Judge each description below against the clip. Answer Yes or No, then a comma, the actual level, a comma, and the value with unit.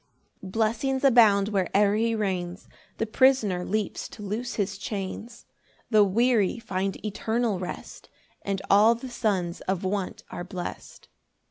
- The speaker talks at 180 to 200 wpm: No, slow, 135 wpm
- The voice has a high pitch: Yes, high, 205 Hz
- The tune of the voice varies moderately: Yes, average, 3.1 semitones